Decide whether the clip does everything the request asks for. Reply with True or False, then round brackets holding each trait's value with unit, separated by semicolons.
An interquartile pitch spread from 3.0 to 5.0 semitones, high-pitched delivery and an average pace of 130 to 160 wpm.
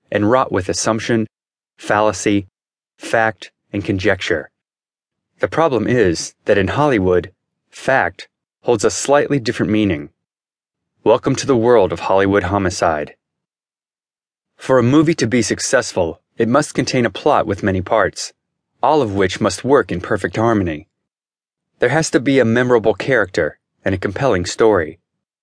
False (3.8 semitones; 110 Hz; 140 wpm)